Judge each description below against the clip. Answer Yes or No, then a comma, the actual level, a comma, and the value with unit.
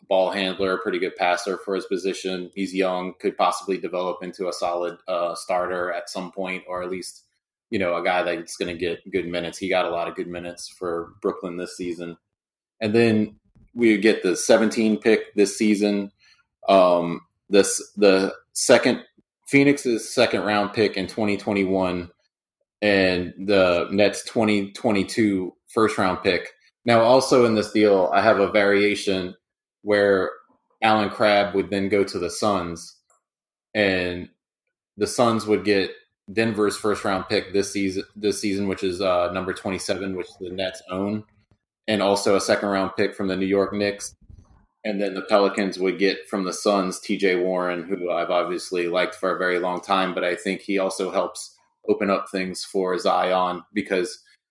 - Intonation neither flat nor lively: No, narrow, 2.3 semitones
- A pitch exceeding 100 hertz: No, very low, 95 Hz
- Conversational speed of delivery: Yes, average, 170 wpm